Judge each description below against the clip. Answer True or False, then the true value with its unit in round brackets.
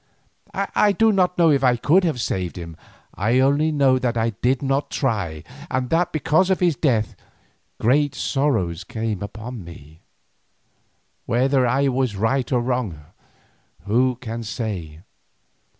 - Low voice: True (125 Hz)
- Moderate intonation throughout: True (4.7 semitones)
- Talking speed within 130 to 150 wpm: True (145 wpm)